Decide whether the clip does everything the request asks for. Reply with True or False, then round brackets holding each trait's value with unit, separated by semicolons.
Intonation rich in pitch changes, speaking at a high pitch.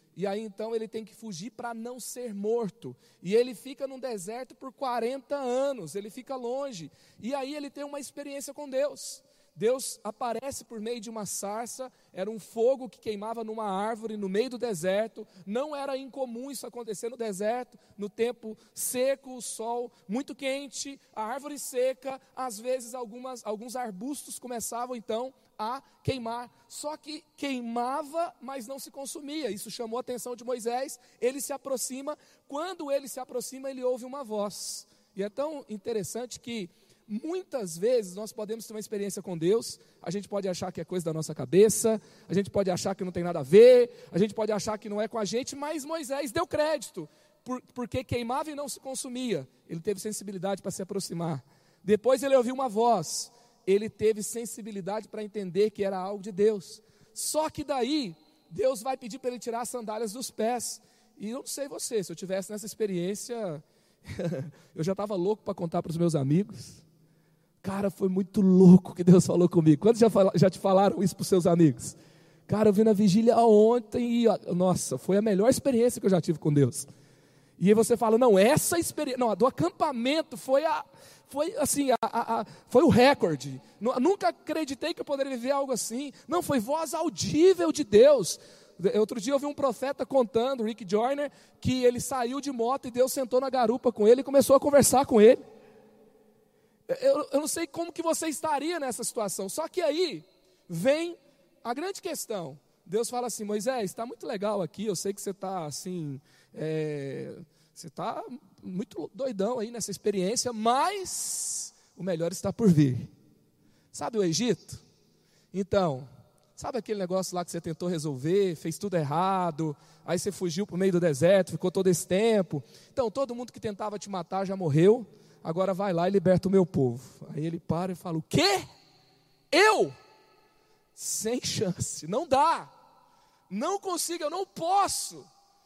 True (5.7 semitones; 225 Hz)